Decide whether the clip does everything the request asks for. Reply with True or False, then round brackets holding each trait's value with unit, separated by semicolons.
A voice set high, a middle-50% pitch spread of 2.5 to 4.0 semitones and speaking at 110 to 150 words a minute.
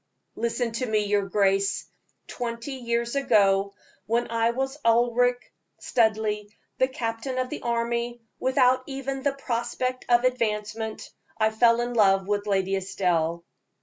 True (235 Hz; 2.9 semitones; 135 wpm)